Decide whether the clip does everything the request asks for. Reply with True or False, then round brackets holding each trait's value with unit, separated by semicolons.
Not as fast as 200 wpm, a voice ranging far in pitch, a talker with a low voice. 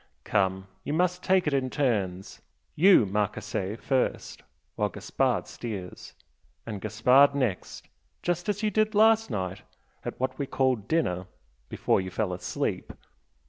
True (140 wpm; 8.7 semitones; 120 Hz)